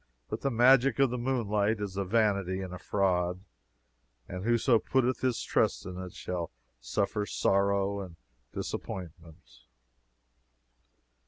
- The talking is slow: Yes, slow, 130 wpm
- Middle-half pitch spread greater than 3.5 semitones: Yes, average, 4.2 semitones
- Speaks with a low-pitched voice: Yes, low, 100 Hz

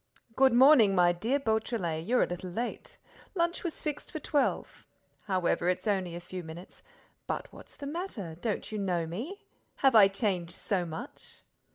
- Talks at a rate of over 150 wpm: Yes, average, 165 wpm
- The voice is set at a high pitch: Yes, high, 205 Hz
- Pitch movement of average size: No, wide, 7.0 semitones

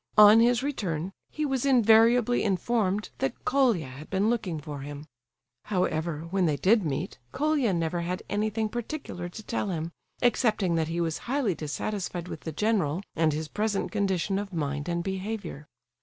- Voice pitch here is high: Yes, high, 195 Hz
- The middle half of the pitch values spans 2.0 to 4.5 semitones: No, wide, 5.4 semitones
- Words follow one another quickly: No, average, 165 wpm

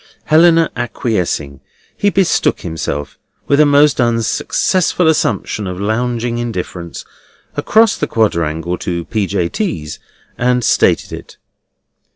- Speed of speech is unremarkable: No, slow, 115 wpm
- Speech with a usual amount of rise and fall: No, wide, 8.7 semitones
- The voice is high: No, low, 115 Hz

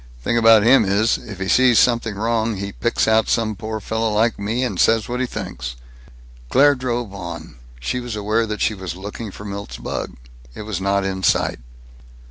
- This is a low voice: Yes, low, 110 Hz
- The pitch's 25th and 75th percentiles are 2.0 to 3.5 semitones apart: Yes, average, 2.7 semitones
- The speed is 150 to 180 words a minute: No, average, 195 wpm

